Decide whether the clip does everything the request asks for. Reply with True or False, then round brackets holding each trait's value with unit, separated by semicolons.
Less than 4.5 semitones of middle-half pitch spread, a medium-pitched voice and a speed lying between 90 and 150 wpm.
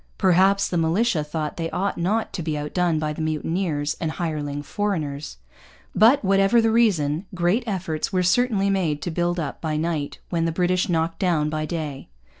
False (4.0 semitones; 170 Hz; 175 wpm)